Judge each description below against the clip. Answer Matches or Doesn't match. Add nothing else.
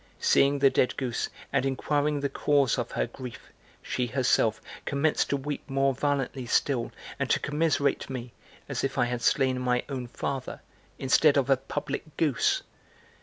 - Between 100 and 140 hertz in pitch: Matches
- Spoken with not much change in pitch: Matches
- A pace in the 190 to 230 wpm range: Doesn't match